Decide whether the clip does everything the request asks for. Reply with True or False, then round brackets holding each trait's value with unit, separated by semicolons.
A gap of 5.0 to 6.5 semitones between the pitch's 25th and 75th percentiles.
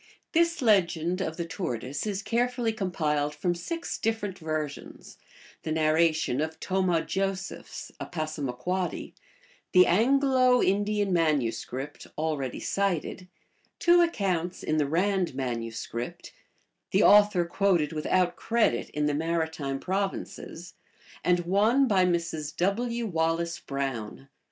False (4.4 semitones)